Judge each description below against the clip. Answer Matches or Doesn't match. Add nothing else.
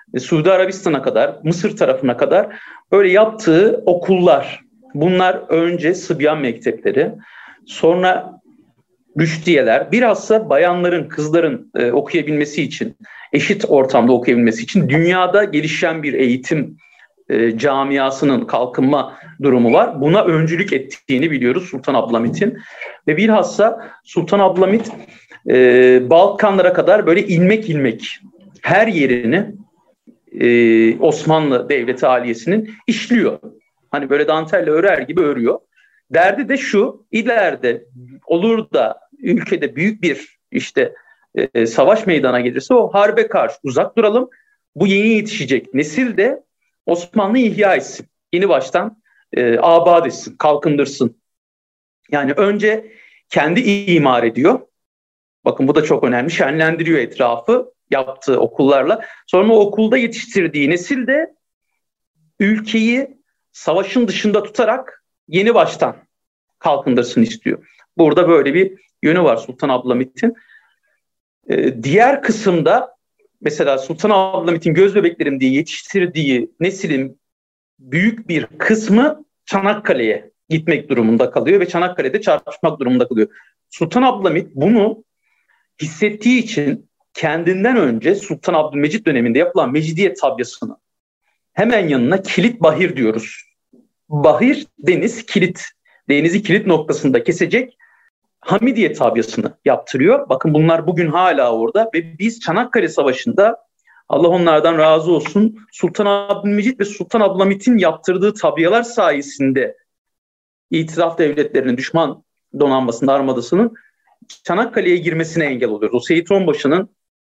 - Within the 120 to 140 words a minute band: Doesn't match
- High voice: Doesn't match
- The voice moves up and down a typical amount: Doesn't match